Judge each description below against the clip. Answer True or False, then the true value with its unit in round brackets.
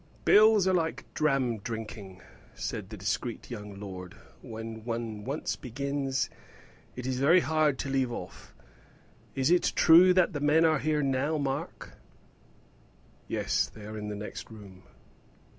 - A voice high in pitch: False (130 Hz)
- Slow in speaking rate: False (145 wpm)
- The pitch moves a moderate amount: False (5.9 semitones)